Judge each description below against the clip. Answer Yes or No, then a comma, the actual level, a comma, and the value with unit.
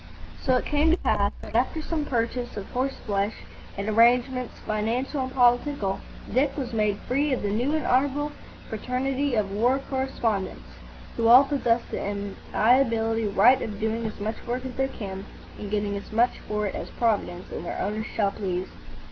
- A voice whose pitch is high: Yes, high, 230 Hz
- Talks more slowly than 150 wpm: No, average, 180 wpm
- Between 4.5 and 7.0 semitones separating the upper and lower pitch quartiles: No, average, 3.9 semitones